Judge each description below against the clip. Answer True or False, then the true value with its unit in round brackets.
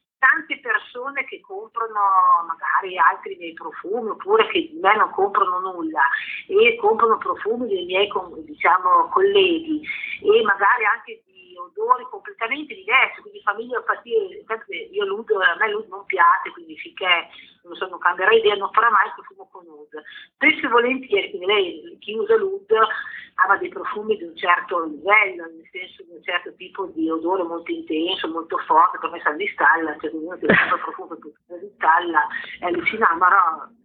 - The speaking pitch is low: False (280 Hz)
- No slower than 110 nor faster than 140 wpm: False (170 wpm)